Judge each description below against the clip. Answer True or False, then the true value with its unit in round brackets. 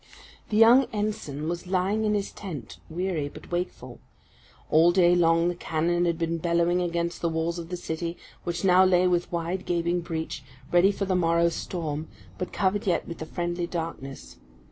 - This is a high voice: False (175 Hz)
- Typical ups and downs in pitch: False (1.6 semitones)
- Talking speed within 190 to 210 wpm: False (180 wpm)